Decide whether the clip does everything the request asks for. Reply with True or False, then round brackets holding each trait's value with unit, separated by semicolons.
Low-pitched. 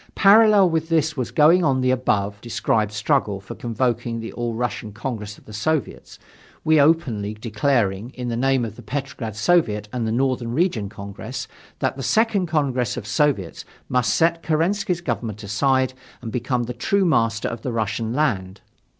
True (125 Hz)